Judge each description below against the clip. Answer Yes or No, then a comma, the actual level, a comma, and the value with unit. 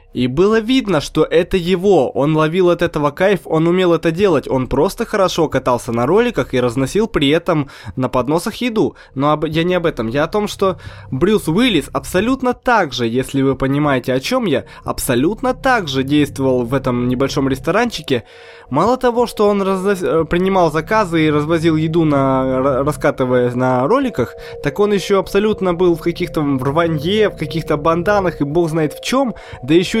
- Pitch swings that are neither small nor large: No, wide, 6.4 semitones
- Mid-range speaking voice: Yes, medium, 165 Hz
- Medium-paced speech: No, fast, 180 wpm